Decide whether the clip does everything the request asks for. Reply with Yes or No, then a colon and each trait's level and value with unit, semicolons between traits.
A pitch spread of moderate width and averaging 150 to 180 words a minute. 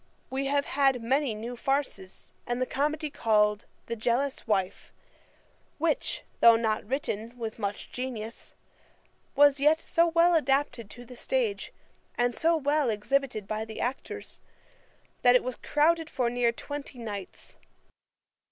No: average, 4.1 semitones; average, 140 wpm